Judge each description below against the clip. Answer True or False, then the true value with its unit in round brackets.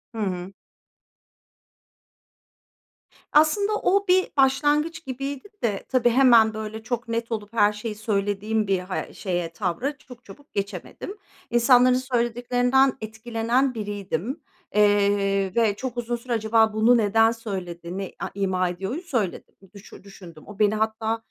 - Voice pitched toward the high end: True (220 Hz)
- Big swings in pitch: False (3.8 semitones)